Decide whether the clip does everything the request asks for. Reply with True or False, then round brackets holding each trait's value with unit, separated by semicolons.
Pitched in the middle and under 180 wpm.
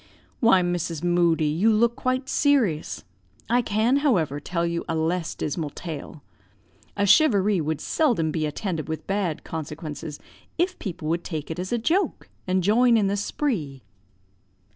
True (180 Hz; 155 wpm)